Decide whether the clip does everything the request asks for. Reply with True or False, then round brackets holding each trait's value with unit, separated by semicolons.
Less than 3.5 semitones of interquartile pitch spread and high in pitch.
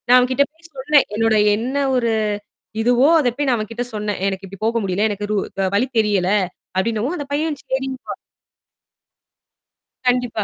False (4.0 semitones; 235 Hz)